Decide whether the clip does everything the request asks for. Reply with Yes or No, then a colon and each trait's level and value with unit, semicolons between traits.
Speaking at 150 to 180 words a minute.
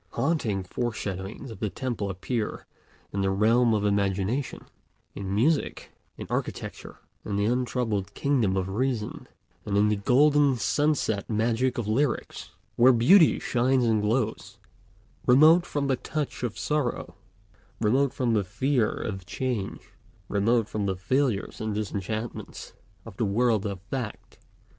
No: average, 140 wpm